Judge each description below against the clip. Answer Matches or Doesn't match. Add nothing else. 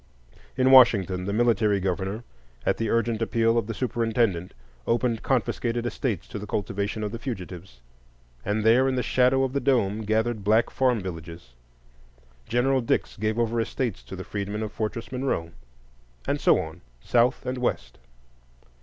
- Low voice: Matches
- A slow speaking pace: Doesn't match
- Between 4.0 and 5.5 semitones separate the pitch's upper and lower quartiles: Doesn't match